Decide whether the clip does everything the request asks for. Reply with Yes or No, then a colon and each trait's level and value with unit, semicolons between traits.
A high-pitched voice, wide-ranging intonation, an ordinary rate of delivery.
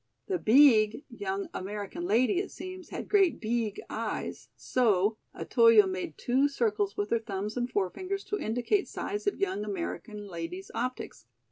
Yes: high, 225 Hz; wide, 5.8 semitones; average, 150 wpm